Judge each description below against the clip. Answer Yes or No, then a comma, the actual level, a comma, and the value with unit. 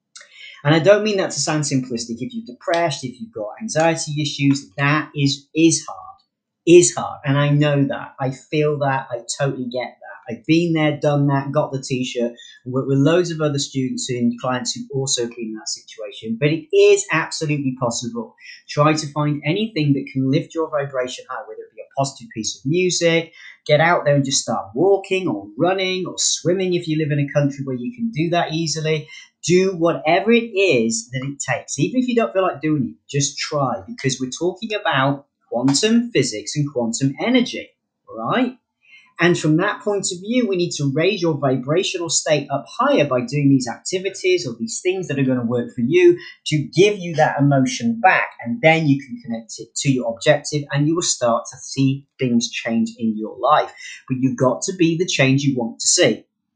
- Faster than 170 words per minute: Yes, fast, 205 wpm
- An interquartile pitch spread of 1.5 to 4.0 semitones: No, average, 4.8 semitones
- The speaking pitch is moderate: Yes, medium, 150 Hz